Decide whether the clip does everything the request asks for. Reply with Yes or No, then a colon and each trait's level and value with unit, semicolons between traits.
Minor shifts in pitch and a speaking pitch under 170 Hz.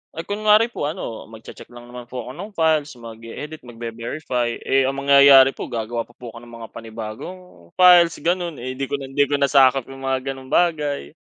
No: average, 4.5 semitones; low, 135 Hz